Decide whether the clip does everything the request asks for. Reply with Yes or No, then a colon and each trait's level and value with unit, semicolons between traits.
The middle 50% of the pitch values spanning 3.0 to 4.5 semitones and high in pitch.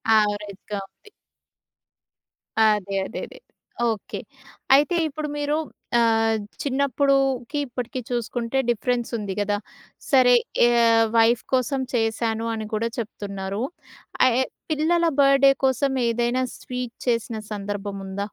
Yes: average, 3.7 semitones; high, 235 Hz